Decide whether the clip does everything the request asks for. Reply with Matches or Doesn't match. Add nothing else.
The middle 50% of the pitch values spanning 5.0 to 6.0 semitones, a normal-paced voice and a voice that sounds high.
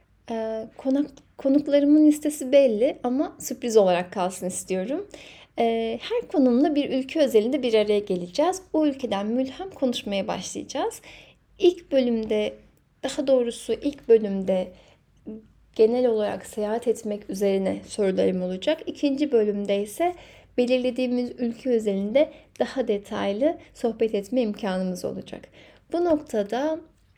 Matches